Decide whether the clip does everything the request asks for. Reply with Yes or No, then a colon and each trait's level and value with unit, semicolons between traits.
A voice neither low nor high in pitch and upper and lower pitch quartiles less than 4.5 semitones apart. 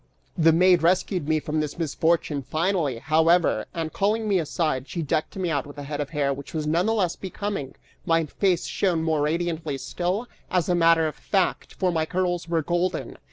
Yes: medium, 165 Hz; average, 2.8 semitones